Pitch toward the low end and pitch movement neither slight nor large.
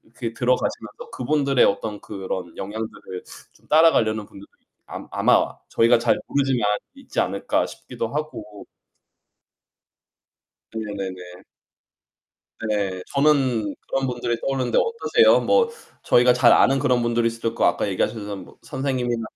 Yes: low, 120 Hz; average, 4.8 semitones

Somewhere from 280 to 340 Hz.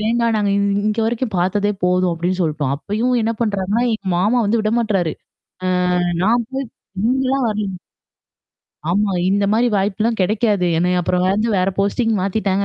No: high, 210 Hz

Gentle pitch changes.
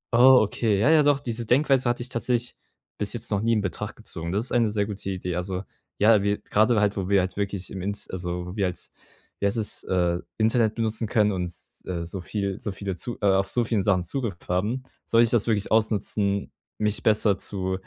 No: average, 3.1 semitones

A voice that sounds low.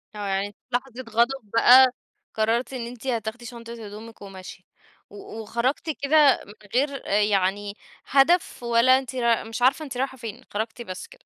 No: high, 235 Hz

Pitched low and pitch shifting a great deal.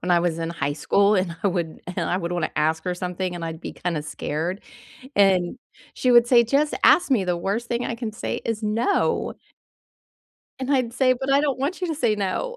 No: high, 200 Hz; wide, 6.1 semitones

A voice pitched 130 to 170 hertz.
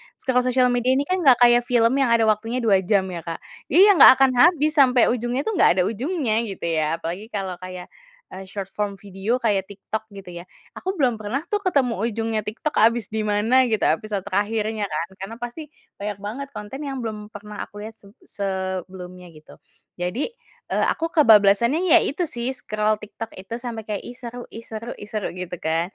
No: high, 220 Hz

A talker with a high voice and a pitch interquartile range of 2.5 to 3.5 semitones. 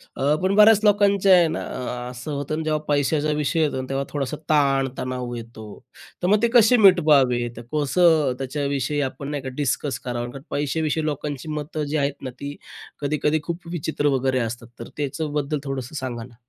No: medium, 145 Hz; average, 2.9 semitones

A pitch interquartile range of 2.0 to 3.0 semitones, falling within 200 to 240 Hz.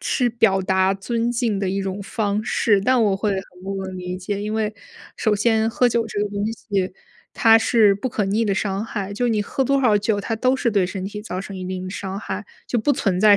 Yes: narrow, 2.6 semitones; high, 205 Hz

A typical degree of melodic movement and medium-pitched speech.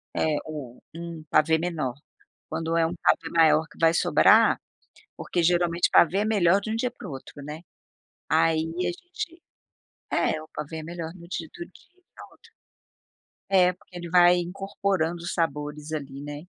No: narrow, 2.3 semitones; medium, 170 Hz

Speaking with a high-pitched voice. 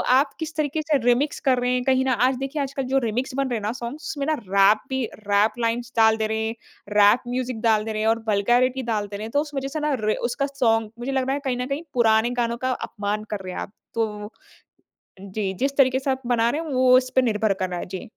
Yes: high, 240 Hz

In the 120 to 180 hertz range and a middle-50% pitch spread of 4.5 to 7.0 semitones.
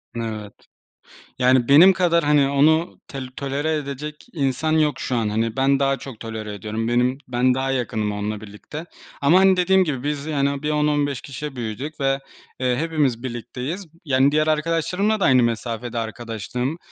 No: low, 135 Hz; average, 4.1 semitones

